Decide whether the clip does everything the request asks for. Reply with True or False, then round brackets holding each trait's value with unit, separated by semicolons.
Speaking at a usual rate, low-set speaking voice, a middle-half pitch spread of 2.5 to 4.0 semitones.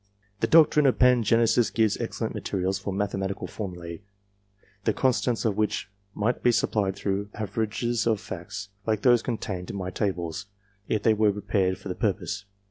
True (160 wpm; 105 Hz; 2.8 semitones)